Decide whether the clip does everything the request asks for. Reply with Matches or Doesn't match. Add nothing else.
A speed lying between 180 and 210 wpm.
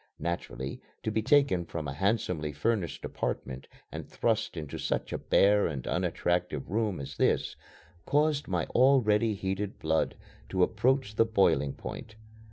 Doesn't match